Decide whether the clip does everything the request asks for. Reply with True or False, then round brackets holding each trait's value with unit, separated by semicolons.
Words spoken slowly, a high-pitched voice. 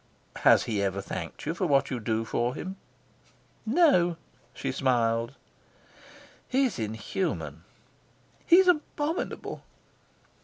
False (105 wpm; 135 Hz)